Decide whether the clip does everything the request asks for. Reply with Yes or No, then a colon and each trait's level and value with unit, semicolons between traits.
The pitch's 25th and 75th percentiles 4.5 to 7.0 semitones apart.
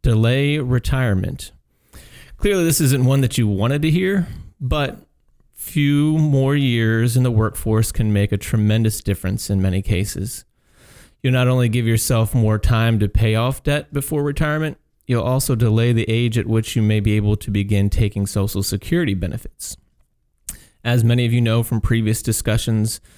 No: average, 3.5 semitones